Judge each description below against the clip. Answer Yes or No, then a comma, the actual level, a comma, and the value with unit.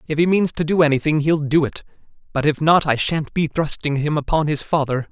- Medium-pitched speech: Yes, medium, 150 Hz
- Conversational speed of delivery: No, fast, 235 wpm